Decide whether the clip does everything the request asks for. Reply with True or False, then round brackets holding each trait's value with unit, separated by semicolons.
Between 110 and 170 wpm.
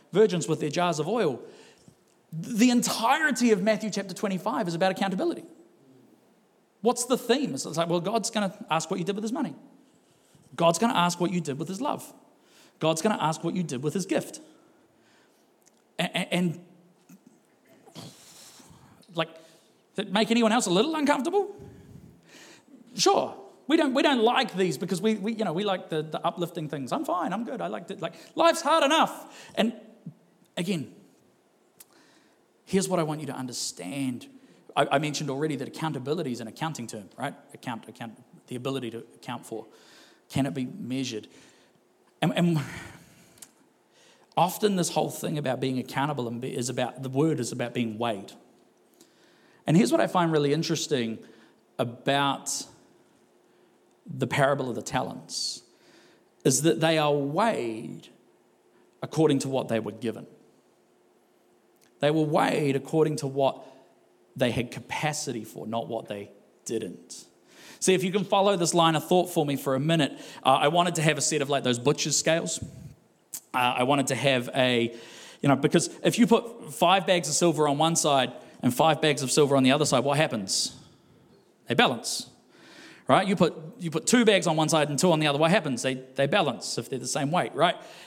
False (180 wpm)